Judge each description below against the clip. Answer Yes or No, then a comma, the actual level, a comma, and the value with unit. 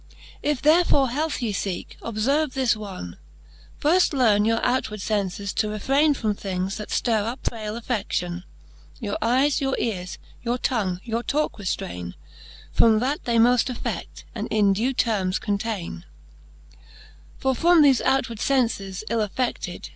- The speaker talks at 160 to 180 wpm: No, average, 145 wpm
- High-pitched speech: Yes, high, 230 Hz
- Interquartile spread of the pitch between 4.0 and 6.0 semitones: Yes, average, 4.5 semitones